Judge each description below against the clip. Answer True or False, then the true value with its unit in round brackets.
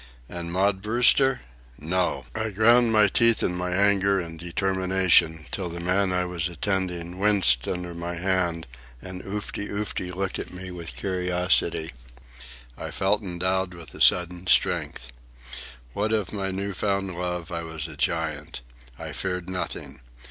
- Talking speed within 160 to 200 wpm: False (150 wpm)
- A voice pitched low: True (90 Hz)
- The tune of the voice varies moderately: False (2.2 semitones)